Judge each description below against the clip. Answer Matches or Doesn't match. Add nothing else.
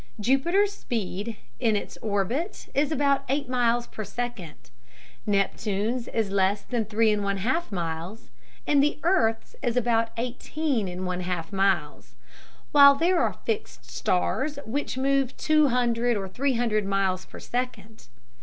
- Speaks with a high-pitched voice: Matches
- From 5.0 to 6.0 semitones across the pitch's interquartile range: Matches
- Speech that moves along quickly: Doesn't match